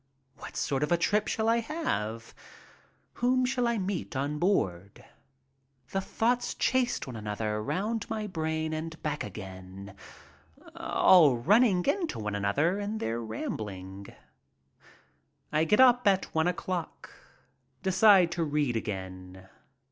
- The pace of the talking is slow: Yes, slow, 130 wpm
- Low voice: No, medium, 160 Hz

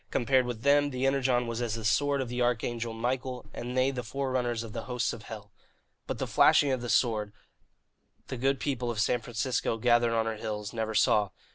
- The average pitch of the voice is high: No, low, 120 Hz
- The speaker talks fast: Yes, fast, 215 wpm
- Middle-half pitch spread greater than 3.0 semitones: No, narrow, 2.4 semitones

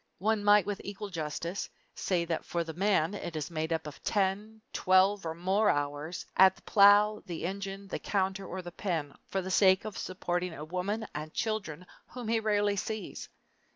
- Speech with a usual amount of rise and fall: Yes, average, 3.4 semitones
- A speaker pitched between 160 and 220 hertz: Yes, high, 190 Hz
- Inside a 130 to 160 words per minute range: No, average, 190 wpm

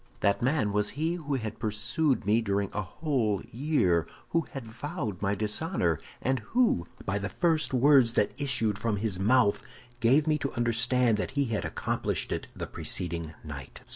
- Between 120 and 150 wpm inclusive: No, average, 170 wpm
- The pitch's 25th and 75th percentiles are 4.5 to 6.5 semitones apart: Yes, wide, 5.6 semitones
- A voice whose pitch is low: Yes, low, 115 Hz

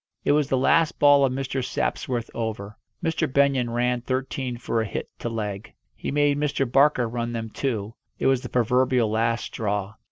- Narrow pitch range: No, average, 3.1 semitones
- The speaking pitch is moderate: No, low, 125 Hz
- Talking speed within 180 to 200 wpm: Yes, average, 185 wpm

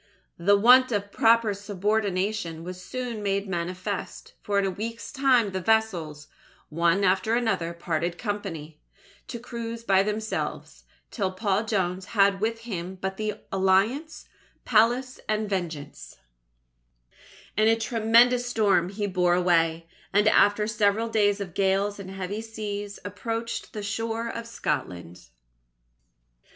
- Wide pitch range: No, average, 3.3 semitones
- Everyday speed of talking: No, slow, 130 wpm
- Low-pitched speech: No, high, 205 Hz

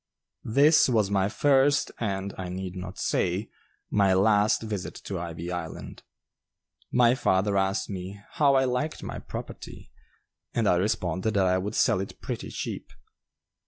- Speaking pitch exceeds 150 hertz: No, low, 100 Hz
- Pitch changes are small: No, average, 3.4 semitones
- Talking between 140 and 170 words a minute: Yes, average, 150 wpm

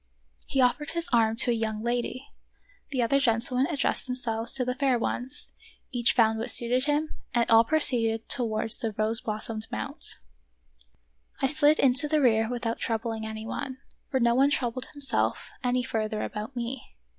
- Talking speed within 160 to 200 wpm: Yes, average, 170 wpm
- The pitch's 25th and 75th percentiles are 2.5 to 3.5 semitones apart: Yes, average, 2.9 semitones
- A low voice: No, high, 240 Hz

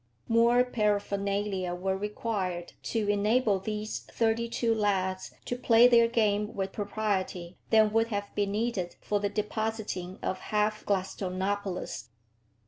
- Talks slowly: Yes, slow, 130 wpm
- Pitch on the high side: Yes, high, 205 Hz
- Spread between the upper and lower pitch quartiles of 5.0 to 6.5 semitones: No, narrow, 2.6 semitones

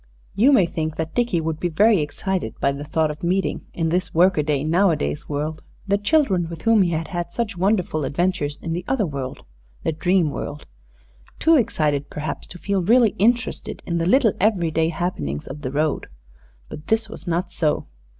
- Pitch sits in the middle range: Yes, medium, 170 Hz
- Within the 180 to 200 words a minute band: Yes, average, 190 wpm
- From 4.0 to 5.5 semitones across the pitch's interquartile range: Yes, average, 4.4 semitones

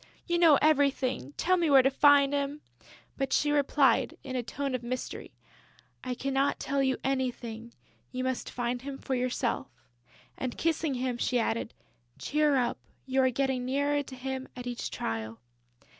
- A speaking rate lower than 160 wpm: No, average, 165 wpm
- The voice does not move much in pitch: Yes, narrow, 2.2 semitones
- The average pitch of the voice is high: Yes, very high, 265 Hz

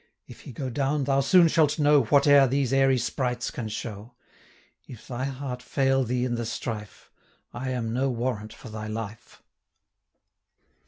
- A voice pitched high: No, low, 125 Hz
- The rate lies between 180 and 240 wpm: No, average, 165 wpm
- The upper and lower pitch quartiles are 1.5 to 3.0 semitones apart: Yes, average, 2.7 semitones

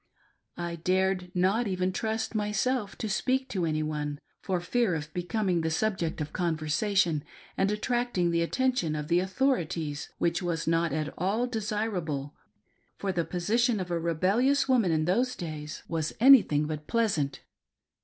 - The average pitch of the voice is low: No, medium, 180 Hz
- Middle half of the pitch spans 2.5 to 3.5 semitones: No, average, 5.2 semitones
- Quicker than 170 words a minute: No, average, 165 wpm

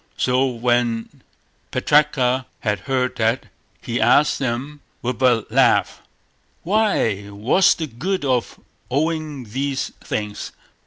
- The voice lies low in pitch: Yes, low, 125 Hz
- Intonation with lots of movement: No, average, 3.8 semitones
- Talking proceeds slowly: Yes, slow, 110 wpm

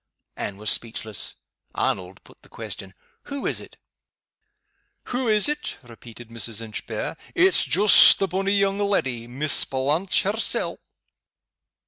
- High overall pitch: No, medium, 145 Hz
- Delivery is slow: Yes, slow, 120 wpm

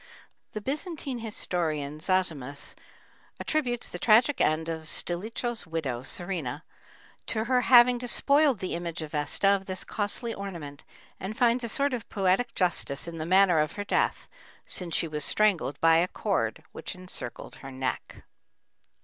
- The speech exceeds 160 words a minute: No, average, 150 wpm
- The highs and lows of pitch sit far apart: Yes, wide, 6.6 semitones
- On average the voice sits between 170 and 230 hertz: Yes, medium, 185 Hz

